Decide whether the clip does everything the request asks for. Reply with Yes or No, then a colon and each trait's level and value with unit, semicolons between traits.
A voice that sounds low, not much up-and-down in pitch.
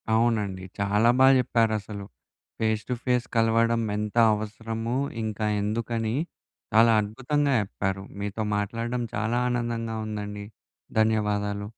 Yes: low, 110 Hz; narrow, 2.1 semitones